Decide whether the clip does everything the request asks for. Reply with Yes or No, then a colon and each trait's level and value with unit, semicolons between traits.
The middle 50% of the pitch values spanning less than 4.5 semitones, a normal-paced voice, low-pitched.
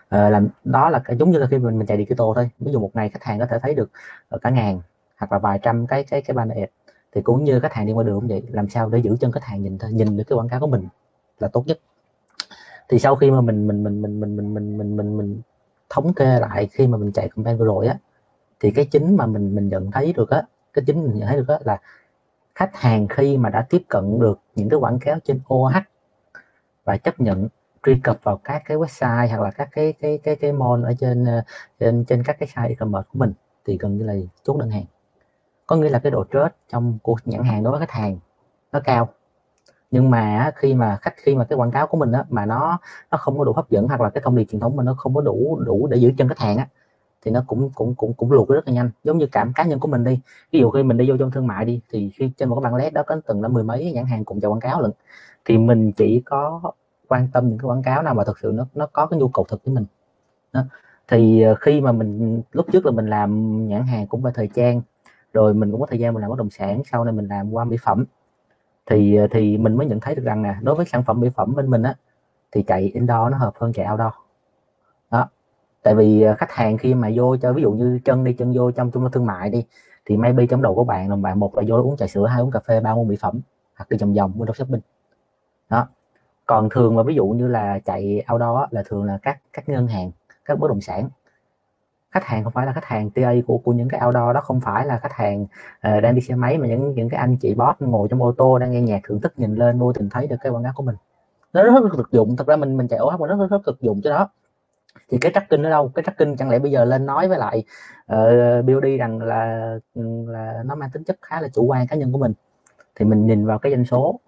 No: average, 3.6 semitones; fast, 275 wpm; low, 120 Hz